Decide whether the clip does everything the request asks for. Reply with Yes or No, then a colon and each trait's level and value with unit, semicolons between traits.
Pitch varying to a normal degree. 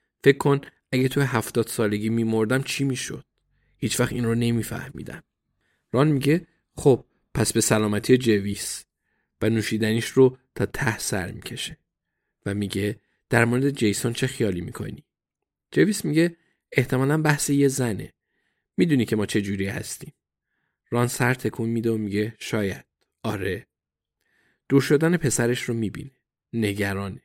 Yes: average, 3.9 semitones